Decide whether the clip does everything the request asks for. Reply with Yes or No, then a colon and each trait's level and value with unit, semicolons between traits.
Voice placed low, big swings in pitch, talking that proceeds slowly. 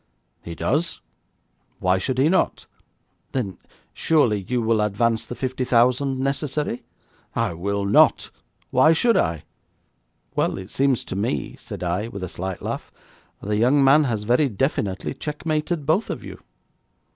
No: low, 120 Hz; wide, 5.7 semitones; average, 145 wpm